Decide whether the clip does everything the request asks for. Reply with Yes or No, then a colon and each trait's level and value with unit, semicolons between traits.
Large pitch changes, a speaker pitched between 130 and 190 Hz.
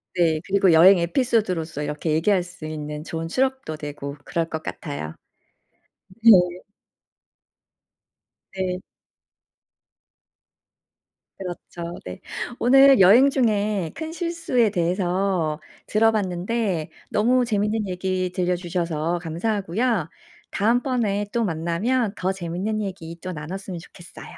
No: average, 4.6 semitones; medium, 185 Hz